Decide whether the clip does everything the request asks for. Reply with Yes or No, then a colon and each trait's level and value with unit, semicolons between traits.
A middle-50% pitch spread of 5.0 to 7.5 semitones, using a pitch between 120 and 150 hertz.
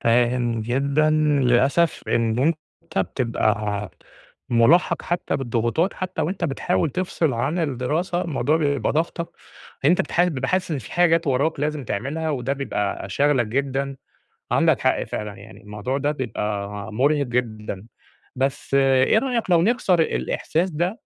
Yes: wide, 5.6 semitones; medium, 140 Hz